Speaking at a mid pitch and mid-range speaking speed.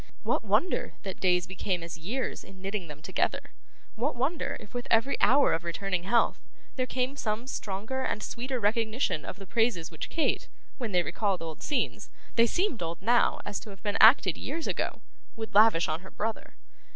No: high, 215 Hz; average, 190 wpm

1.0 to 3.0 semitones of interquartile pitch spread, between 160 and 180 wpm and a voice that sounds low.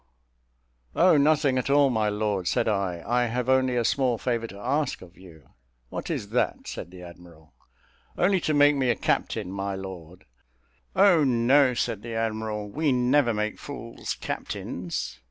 No: wide, 5.5 semitones; average, 165 wpm; low, 115 Hz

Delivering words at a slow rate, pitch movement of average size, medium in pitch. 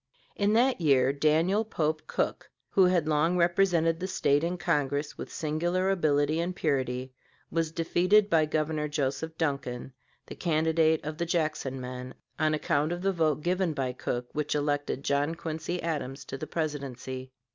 No: average, 160 wpm; average, 3.2 semitones; medium, 155 Hz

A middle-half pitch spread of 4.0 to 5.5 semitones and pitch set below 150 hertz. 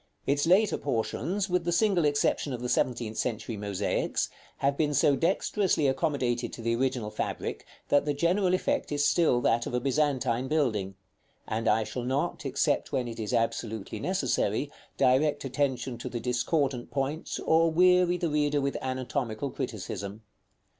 Yes: average, 4.5 semitones; low, 135 Hz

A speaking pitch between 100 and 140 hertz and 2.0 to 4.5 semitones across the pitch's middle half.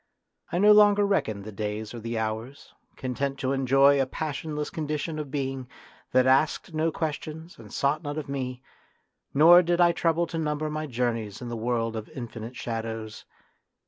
No: low, 135 Hz; average, 4.9 semitones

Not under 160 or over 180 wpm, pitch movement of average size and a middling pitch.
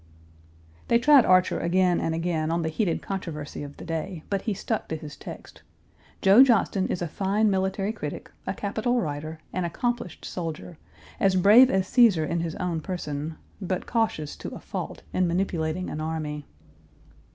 Yes: average, 170 wpm; average, 3.8 semitones; medium, 180 Hz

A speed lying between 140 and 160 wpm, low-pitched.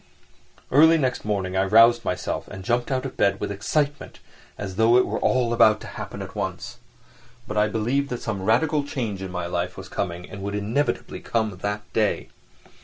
No: average, 190 wpm; low, 110 Hz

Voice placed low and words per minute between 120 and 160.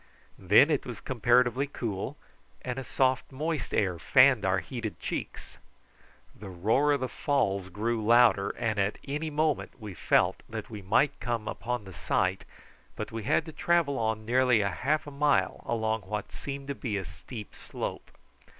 No: low, 120 Hz; average, 170 wpm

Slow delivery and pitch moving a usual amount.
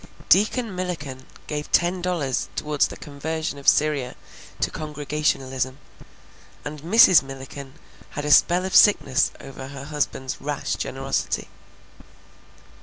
Yes: slow, 115 wpm; average, 3.2 semitones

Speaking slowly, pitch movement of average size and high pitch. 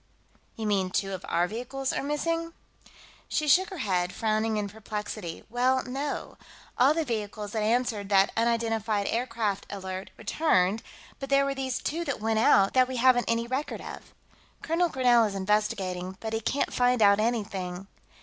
No: average, 170 wpm; average, 4.3 semitones; high, 225 Hz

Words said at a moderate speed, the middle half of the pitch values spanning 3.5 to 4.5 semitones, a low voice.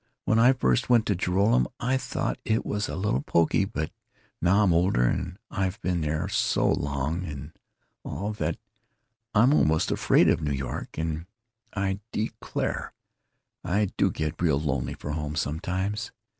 No: average, 155 wpm; average, 5.0 semitones; very low, 90 Hz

